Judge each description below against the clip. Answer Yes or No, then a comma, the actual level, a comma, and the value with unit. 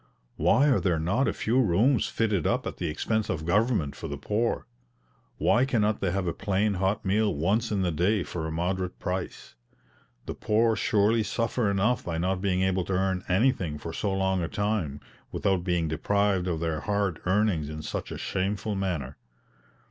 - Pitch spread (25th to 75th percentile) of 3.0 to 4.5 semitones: Yes, average, 3.5 semitones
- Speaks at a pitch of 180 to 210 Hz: No, very low, 95 Hz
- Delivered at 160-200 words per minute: Yes, average, 185 wpm